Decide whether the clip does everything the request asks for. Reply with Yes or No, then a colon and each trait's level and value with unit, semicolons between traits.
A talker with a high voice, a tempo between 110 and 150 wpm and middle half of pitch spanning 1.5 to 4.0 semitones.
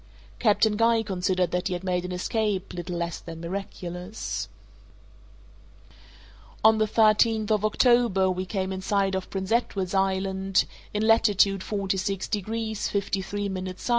Yes: high, 195 Hz; slow, 135 wpm; narrow, 2.6 semitones